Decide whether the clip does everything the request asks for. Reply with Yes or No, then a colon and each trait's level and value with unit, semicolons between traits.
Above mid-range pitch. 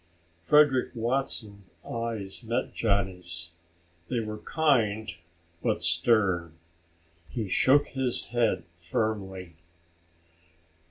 No: low, 110 Hz